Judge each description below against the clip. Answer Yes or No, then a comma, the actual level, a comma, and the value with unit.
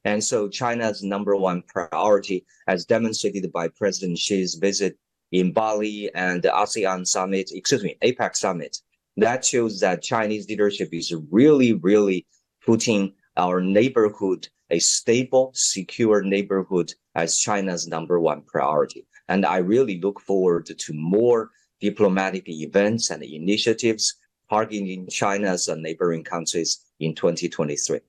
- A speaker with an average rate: No, slow, 125 wpm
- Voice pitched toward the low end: Yes, low, 100 Hz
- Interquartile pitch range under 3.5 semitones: Yes, average, 3.1 semitones